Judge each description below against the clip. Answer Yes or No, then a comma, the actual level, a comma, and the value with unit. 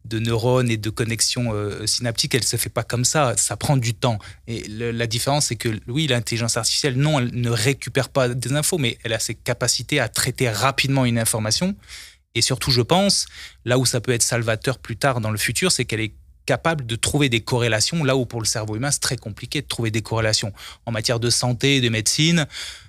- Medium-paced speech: No, fast, 225 wpm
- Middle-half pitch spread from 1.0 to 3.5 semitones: Yes, average, 2.8 semitones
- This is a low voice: Yes, low, 120 Hz